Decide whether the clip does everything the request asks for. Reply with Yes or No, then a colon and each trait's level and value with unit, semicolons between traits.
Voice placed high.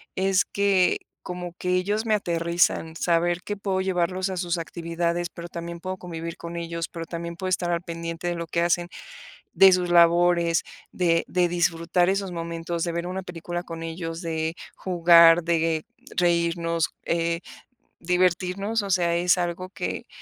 No: medium, 175 Hz